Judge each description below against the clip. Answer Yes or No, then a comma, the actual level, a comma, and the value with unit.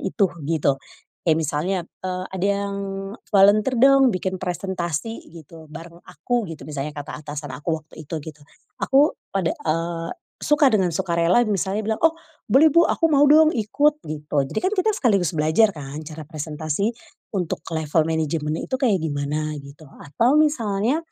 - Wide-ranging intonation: Yes, wide, 6.5 semitones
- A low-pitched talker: No, medium, 175 Hz